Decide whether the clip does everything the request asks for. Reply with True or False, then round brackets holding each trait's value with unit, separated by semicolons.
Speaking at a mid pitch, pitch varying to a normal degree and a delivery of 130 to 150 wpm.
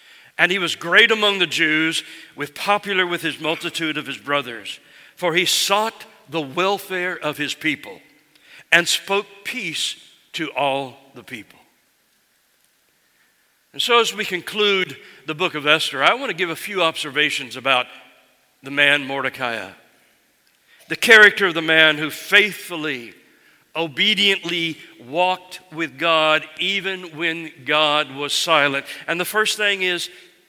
True (165 Hz; 3.9 semitones; 140 wpm)